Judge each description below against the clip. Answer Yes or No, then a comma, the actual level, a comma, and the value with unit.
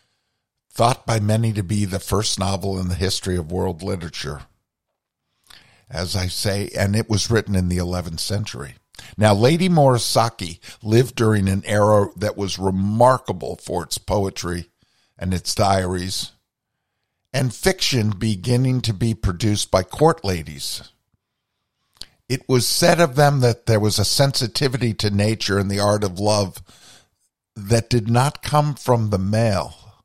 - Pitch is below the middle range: Yes, low, 105 Hz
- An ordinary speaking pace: Yes, average, 150 wpm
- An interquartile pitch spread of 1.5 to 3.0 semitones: No, average, 3.5 semitones